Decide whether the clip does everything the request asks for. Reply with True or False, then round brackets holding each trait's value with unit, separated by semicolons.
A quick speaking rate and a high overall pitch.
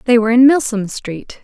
True (210 wpm; 235 Hz)